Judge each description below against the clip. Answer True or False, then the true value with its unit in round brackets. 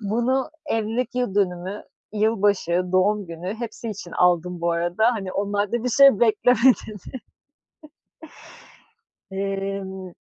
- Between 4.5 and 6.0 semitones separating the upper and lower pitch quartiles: False (3.4 semitones)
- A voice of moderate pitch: False (205 Hz)